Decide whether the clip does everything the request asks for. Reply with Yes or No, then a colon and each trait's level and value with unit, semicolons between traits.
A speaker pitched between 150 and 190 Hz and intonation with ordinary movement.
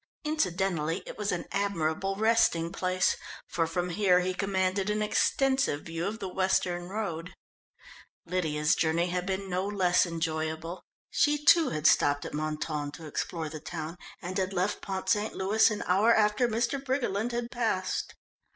Yes: medium, 185 Hz; average, 4.0 semitones